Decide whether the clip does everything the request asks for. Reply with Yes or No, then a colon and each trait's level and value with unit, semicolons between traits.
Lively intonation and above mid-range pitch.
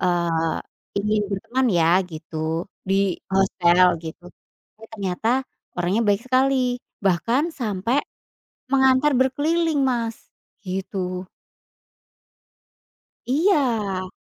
Yes: wide, 6.1 semitones; high, 205 Hz